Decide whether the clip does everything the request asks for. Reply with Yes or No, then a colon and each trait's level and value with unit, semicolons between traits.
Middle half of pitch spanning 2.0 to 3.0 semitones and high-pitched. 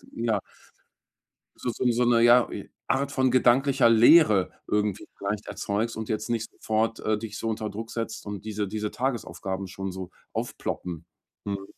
No: average, 2.7 semitones; low, 110 Hz